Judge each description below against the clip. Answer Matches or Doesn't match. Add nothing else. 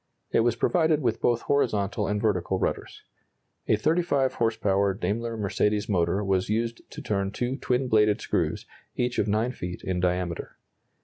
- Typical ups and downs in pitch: Matches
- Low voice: Matches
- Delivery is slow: Doesn't match